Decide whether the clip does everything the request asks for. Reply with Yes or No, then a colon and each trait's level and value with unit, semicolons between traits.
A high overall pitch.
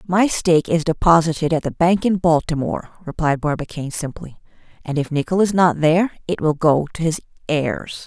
No: medium, 160 Hz